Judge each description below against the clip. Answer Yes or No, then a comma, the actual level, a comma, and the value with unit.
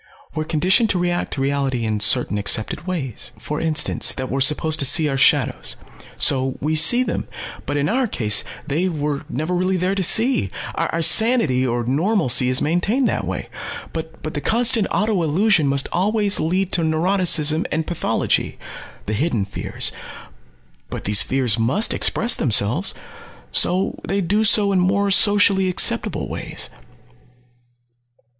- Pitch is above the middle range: No, medium, 160 Hz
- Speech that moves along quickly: No, average, 150 wpm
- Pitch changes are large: Yes, wide, 6.2 semitones